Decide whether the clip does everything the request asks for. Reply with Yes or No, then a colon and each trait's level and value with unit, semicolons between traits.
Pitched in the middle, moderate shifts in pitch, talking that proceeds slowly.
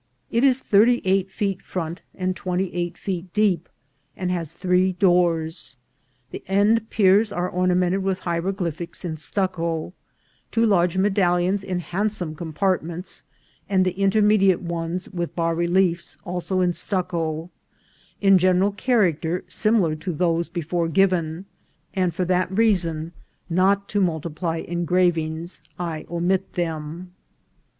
No: medium, 180 Hz; narrow, 2.3 semitones; slow, 130 wpm